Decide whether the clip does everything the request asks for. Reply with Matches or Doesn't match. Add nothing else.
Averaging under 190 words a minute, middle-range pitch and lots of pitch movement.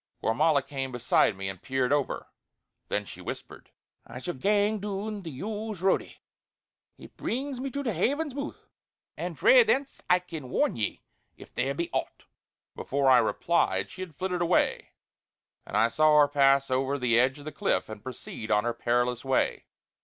Matches